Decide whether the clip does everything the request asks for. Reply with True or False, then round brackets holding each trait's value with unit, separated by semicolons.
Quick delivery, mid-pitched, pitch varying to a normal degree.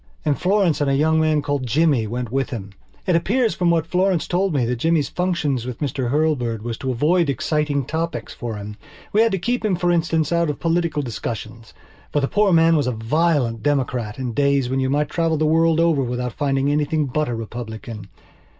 True (215 wpm; 145 Hz; 5.0 semitones)